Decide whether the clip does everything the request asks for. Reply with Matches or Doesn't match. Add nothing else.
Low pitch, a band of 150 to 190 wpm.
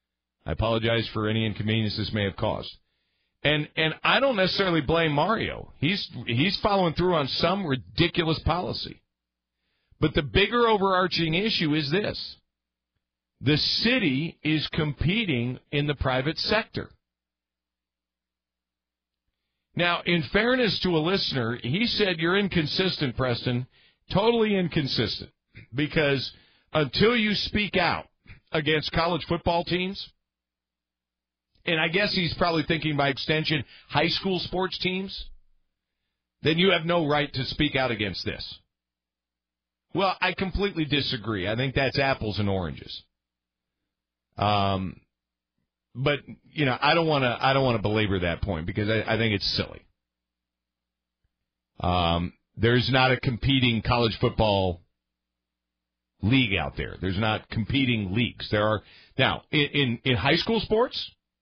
Doesn't match